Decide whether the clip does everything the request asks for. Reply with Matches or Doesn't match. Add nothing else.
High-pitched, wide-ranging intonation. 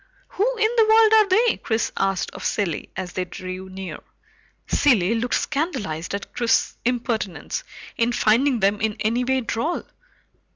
Matches